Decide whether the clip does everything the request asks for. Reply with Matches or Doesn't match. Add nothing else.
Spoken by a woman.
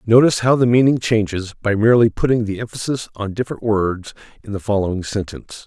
Doesn't match